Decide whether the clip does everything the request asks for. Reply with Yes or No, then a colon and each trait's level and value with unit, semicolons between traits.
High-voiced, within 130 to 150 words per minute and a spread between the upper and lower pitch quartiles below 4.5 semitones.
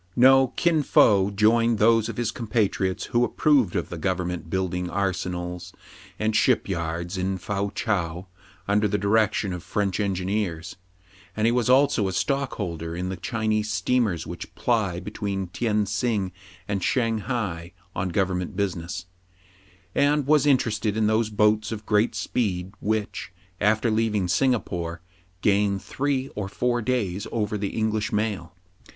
No: low, 105 Hz; average, 145 wpm; average, 3.6 semitones